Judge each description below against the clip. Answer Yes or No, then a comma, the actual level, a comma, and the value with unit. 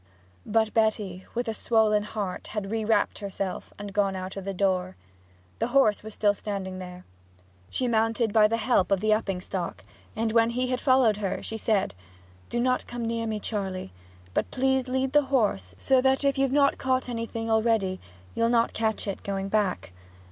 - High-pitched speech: Yes, high, 220 Hz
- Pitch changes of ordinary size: Yes, average, 3.3 semitones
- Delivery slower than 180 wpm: No, average, 185 wpm